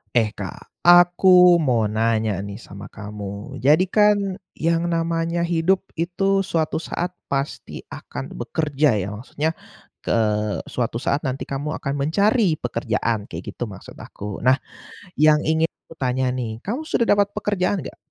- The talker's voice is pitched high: No, medium, 145 Hz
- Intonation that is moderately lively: No, wide, 7.1 semitones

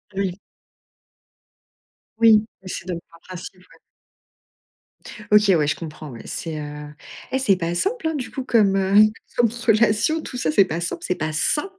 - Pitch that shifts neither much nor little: No, wide, 5.7 semitones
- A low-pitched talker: No, high, 190 Hz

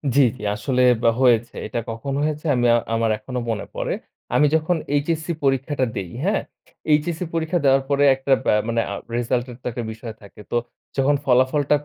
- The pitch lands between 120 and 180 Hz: Yes, low, 135 Hz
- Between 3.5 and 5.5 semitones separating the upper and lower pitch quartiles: Yes, average, 4.0 semitones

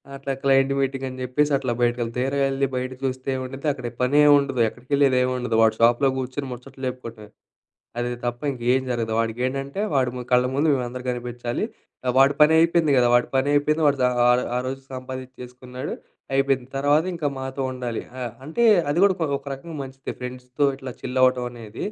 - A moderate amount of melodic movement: No, narrow, 1.8 semitones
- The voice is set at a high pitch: No, low, 130 Hz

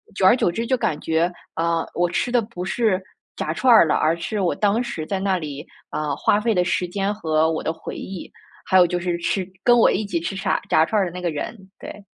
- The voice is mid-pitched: Yes, medium, 180 Hz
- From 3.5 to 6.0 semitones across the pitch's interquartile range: Yes, average, 3.8 semitones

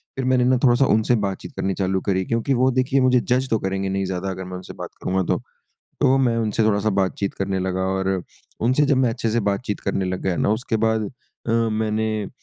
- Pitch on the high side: No, low, 110 Hz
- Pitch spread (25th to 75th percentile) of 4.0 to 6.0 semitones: Yes, average, 4.4 semitones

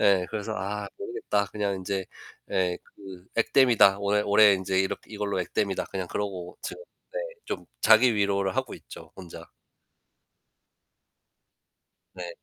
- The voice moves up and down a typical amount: No, narrow, 1.8 semitones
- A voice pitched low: Yes, low, 100 Hz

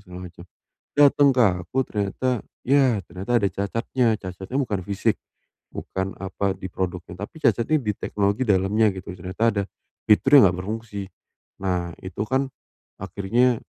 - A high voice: No, low, 100 Hz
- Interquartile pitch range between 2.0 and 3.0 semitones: No, average, 4.3 semitones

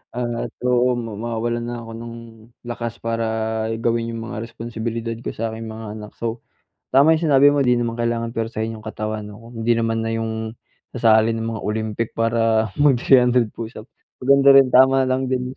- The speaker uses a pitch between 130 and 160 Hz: No, low, 115 Hz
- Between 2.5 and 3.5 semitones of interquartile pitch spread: No, narrow, 1.6 semitones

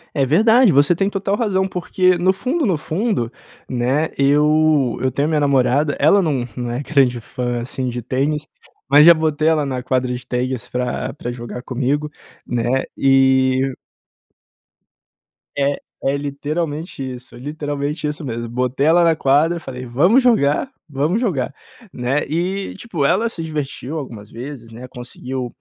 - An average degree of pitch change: Yes, average, 4.1 semitones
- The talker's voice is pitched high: No, medium, 140 Hz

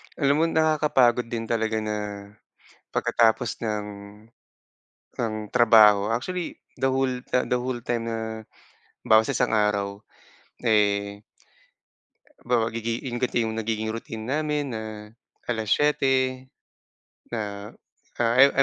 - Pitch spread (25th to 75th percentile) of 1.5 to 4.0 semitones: Yes, average, 2.9 semitones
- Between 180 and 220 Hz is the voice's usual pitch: No, low, 115 Hz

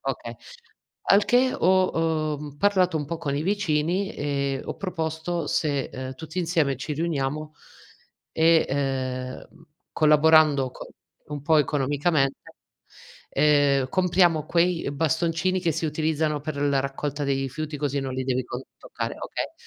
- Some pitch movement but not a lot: Yes, average, 3.0 semitones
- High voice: No, medium, 150 Hz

